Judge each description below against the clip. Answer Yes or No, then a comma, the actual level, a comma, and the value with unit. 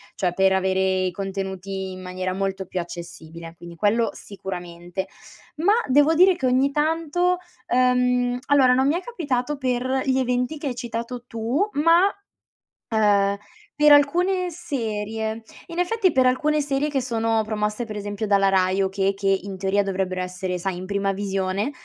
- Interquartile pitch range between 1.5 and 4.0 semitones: No, wide, 6.2 semitones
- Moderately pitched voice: No, high, 220 Hz